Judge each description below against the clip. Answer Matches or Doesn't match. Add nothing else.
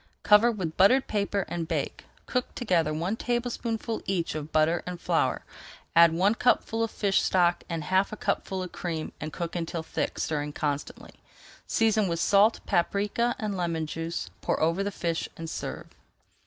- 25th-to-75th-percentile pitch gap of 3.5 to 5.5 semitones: Matches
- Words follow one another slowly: Doesn't match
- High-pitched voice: Doesn't match